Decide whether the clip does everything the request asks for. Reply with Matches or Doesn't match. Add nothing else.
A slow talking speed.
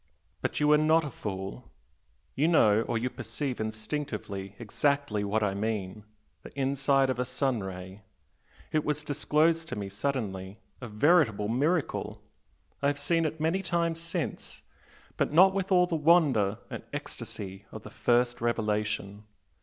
Doesn't match